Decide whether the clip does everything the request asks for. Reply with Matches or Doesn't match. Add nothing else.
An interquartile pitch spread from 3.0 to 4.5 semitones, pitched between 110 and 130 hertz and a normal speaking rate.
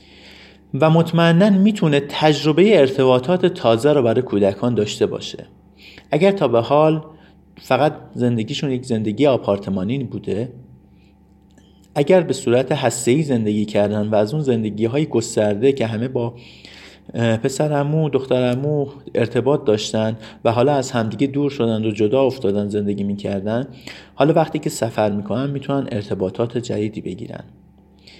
Doesn't match